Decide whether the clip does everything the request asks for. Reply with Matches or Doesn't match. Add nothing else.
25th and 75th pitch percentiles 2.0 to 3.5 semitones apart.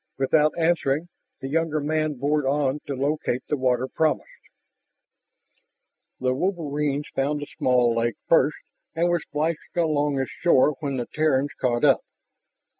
Matches